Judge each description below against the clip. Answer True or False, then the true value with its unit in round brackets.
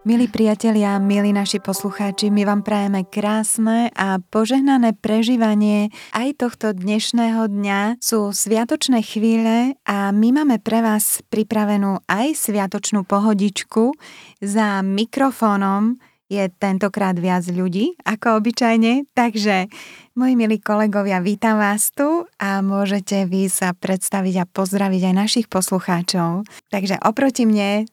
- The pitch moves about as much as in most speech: False (2.3 semitones)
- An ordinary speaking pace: True (120 wpm)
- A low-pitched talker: False (210 Hz)